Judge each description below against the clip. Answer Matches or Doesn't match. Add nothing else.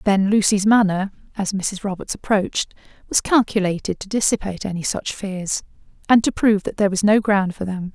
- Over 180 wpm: Matches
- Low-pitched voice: Doesn't match